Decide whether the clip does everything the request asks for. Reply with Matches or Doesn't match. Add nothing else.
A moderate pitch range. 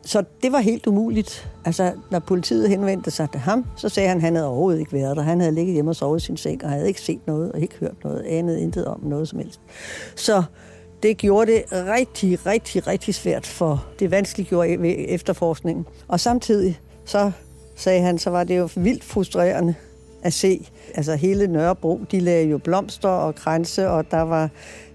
Matches